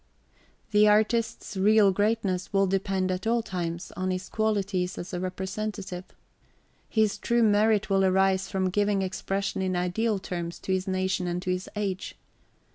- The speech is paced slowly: No, average, 155 wpm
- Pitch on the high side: Yes, high, 195 Hz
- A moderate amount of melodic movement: No, narrow, 2.1 semitones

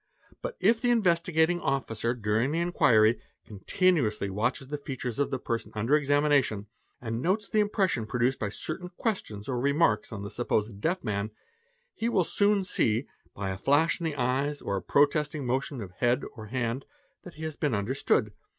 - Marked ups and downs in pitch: Yes, wide, 6.6 semitones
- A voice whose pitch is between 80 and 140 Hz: Yes, low, 135 Hz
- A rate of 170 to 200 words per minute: Yes, average, 185 wpm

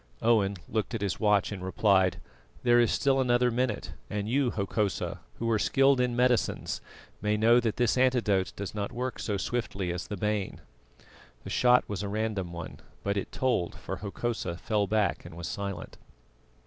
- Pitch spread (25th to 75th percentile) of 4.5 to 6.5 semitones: No, average, 3.5 semitones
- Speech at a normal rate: Yes, average, 175 wpm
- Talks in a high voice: No, low, 105 Hz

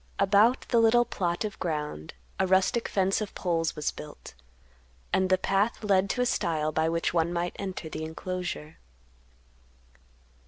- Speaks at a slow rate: No, average, 155 wpm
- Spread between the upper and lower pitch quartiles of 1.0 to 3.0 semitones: No, average, 3.6 semitones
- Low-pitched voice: No, medium, 185 Hz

